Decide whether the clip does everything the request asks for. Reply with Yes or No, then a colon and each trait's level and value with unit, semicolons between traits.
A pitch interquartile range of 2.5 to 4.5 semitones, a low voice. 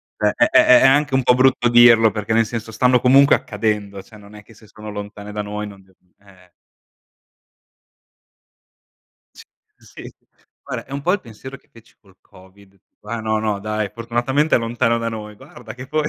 Yes: average, 2.8 semitones; low, 110 Hz